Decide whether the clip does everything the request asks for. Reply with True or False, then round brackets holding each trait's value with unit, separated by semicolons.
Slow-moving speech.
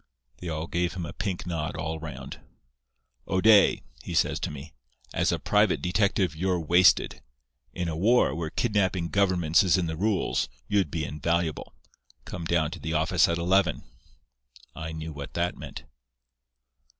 False (155 wpm)